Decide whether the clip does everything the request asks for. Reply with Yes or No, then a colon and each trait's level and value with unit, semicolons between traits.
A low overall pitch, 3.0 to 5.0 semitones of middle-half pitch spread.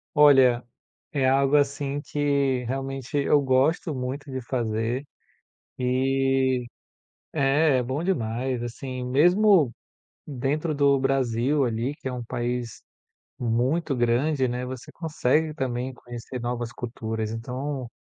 No: low, 130 Hz; narrow, 2.6 semitones